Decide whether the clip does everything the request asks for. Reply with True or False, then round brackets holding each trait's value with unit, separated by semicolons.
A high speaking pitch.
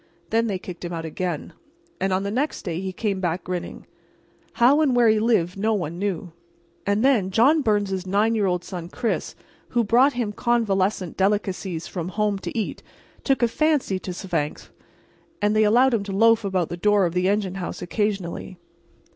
True (200 Hz)